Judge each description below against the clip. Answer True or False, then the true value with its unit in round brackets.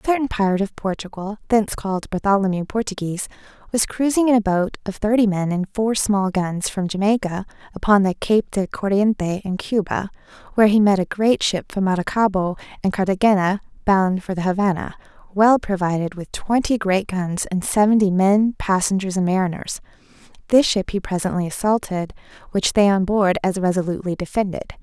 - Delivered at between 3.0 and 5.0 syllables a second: False (5.5 syllables/s)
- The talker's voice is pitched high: True (195 Hz)